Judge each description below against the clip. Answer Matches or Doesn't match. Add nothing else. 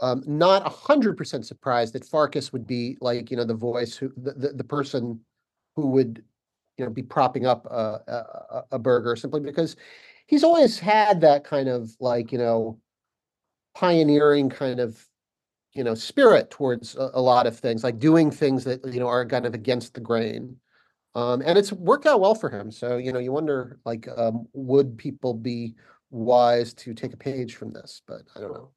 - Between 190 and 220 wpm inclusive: Matches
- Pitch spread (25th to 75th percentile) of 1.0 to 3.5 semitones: Matches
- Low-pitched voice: Matches